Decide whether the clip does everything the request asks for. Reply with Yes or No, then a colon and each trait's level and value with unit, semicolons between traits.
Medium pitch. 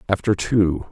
No: very low, 95 Hz